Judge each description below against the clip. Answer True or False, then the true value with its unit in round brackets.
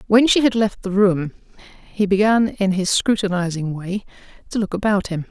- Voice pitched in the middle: False (200 Hz)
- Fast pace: False (180 wpm)